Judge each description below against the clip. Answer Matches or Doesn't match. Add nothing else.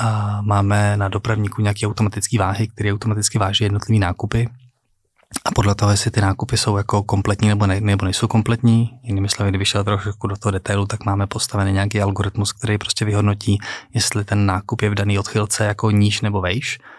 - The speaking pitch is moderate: Doesn't match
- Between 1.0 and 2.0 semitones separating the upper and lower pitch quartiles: Matches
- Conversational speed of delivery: Doesn't match